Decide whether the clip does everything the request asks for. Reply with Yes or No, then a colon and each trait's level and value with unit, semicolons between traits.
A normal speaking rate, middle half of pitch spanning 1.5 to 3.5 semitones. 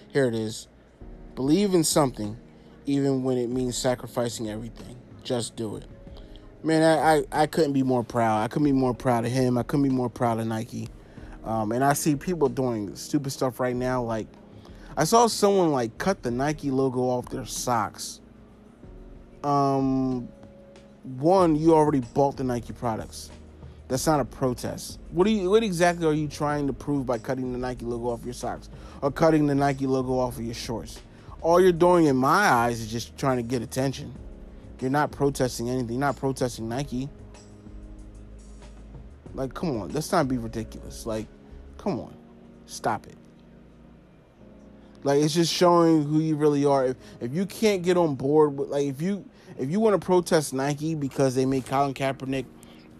No: average, 180 wpm; average, 4.6 semitones